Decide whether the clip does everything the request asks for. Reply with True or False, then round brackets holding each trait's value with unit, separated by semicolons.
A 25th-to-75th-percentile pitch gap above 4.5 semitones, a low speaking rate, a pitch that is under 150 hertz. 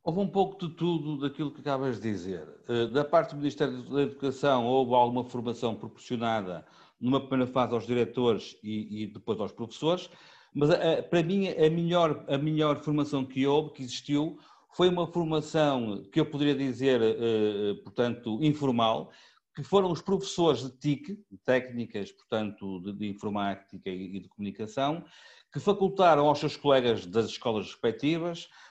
False (5.2 semitones; 165 wpm; 135 Hz)